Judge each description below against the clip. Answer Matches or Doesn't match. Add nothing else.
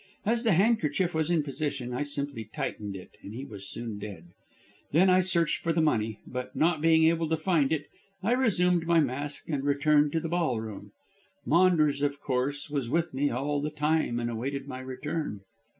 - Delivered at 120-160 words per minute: Doesn't match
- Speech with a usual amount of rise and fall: Matches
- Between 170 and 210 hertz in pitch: Doesn't match